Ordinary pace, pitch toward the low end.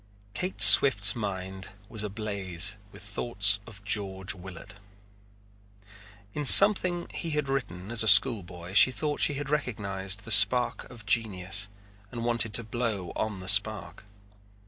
Yes: average, 145 wpm; low, 105 Hz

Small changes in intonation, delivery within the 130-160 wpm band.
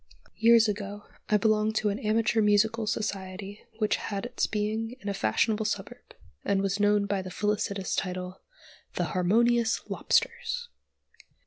Yes: narrow, 1.9 semitones; average, 140 wpm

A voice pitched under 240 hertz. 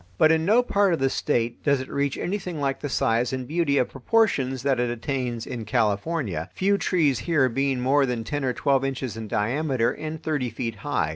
Yes: low, 135 Hz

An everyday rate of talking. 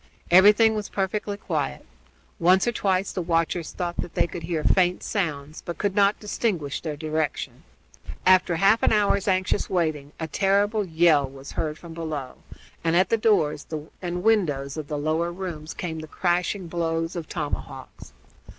Yes: average, 165 wpm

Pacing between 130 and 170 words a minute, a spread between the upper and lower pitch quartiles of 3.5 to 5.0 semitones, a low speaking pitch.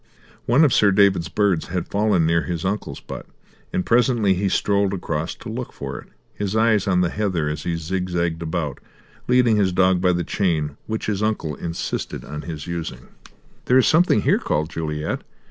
No: average, 185 wpm; average, 4.2 semitones; very low, 95 Hz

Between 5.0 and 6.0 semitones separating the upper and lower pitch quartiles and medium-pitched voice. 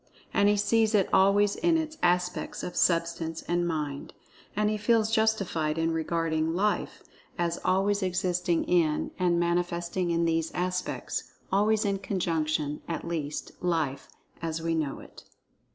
No: average, 3.3 semitones; medium, 175 Hz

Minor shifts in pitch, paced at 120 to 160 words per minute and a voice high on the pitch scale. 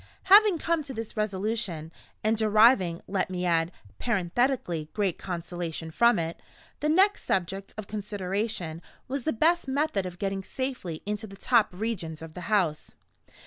No: average, 5.2 semitones; average, 150 wpm; high, 200 Hz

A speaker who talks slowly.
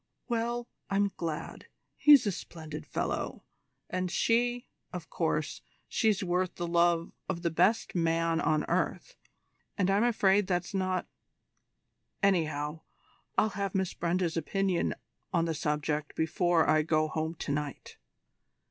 Yes: slow, 130 wpm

